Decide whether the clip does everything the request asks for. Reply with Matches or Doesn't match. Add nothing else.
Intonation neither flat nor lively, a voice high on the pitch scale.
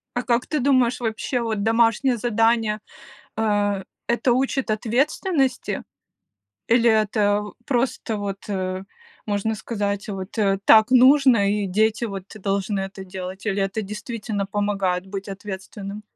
Matches